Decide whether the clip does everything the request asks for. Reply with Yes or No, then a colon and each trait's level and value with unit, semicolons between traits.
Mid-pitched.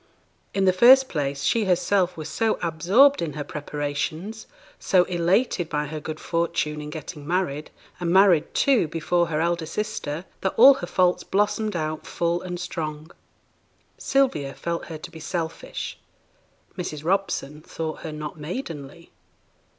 Yes: medium, 170 Hz